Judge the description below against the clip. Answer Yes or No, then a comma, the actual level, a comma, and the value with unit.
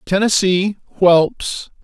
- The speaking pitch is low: No, high, 190 Hz